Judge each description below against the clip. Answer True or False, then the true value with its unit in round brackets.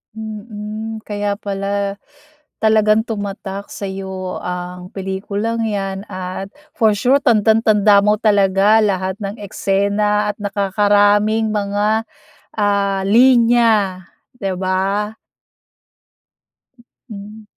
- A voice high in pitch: True (205 Hz)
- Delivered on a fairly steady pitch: True (1.8 semitones)